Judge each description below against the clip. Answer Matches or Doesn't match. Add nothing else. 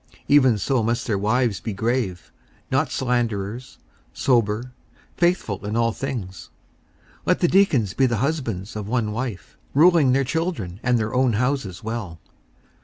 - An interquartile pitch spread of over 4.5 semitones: Doesn't match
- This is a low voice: Matches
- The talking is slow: Doesn't match